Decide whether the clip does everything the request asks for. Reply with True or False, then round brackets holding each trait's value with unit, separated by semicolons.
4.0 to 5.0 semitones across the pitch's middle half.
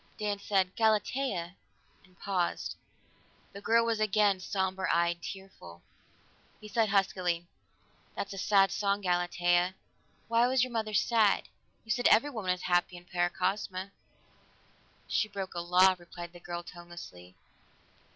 False (3.2 semitones)